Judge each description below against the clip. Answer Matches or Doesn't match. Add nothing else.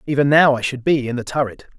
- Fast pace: Matches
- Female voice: Doesn't match